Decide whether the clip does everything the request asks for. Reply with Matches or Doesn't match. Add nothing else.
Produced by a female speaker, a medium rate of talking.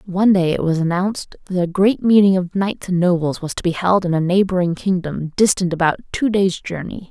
Doesn't match